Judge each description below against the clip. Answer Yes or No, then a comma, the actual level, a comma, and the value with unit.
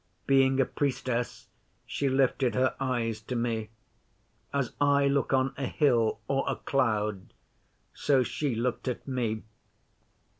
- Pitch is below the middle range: Yes, low, 130 Hz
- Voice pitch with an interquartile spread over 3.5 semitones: No, average, 2.7 semitones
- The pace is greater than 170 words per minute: No, slow, 135 wpm